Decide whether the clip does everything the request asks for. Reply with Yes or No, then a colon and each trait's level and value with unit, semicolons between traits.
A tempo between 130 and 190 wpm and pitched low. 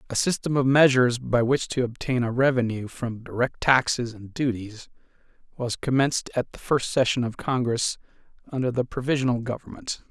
Yes: average, 160 wpm; low, 125 Hz